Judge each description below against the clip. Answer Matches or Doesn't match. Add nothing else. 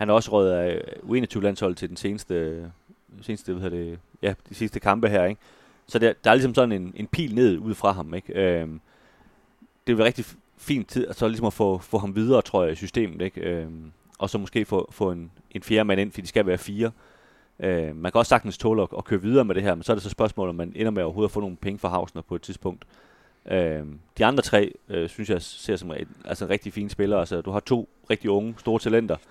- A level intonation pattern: Doesn't match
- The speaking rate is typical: Doesn't match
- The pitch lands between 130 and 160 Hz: Doesn't match